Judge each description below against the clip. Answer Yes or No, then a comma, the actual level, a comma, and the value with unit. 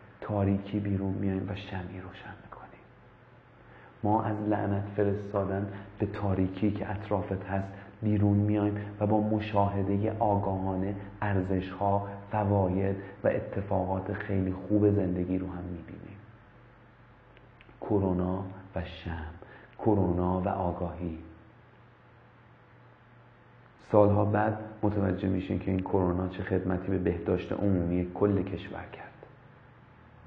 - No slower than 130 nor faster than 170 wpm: No, slow, 105 wpm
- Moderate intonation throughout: No, narrow, 2.0 semitones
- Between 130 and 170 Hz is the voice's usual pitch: No, low, 100 Hz